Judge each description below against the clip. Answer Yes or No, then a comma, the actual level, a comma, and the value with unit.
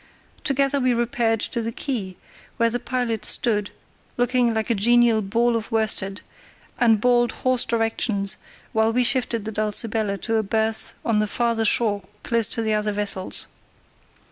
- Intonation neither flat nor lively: No, narrow, 2.1 semitones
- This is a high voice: Yes, high, 225 Hz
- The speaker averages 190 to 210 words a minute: No, average, 160 wpm